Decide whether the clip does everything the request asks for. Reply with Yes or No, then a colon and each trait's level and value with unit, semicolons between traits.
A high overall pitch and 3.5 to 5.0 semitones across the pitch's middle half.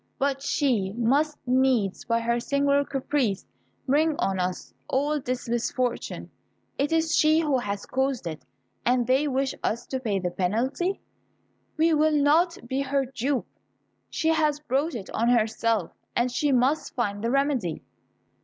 Yes: very high, 260 Hz; average, 3.8 semitones